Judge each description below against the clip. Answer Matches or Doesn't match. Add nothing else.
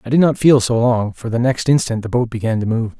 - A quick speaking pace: Matches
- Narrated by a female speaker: Doesn't match